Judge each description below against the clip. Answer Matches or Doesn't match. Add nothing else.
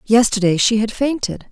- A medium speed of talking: Matches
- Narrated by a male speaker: Doesn't match